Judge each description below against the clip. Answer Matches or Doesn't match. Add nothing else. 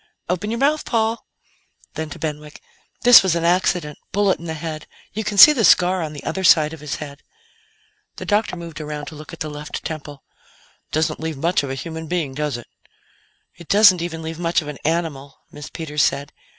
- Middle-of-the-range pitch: Matches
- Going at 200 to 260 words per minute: Matches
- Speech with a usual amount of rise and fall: Matches